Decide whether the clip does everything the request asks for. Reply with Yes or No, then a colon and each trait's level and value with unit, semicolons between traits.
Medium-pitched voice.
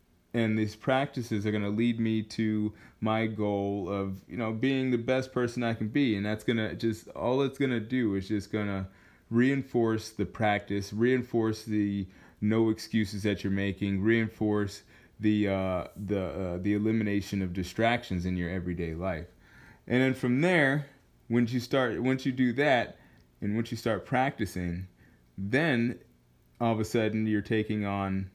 No: low, 110 Hz